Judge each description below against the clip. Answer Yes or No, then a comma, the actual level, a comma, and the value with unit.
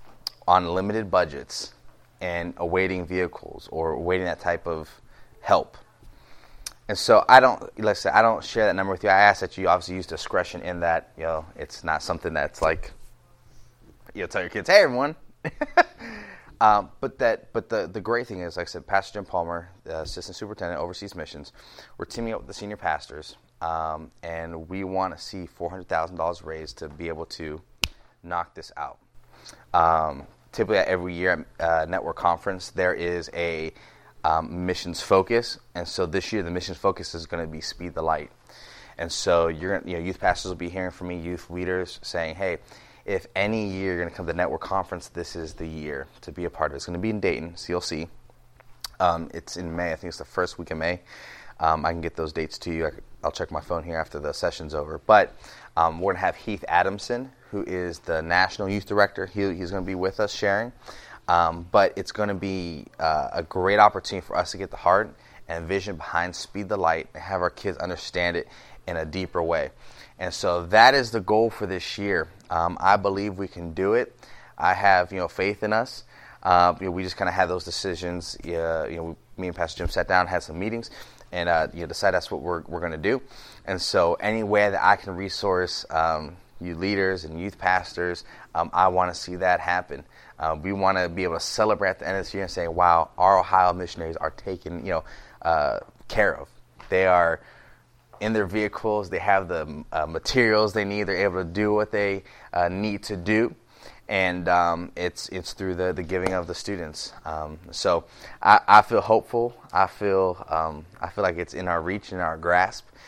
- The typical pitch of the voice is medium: No, very low, 90 Hz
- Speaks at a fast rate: Yes, fast, 215 wpm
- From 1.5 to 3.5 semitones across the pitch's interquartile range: Yes, average, 2.9 semitones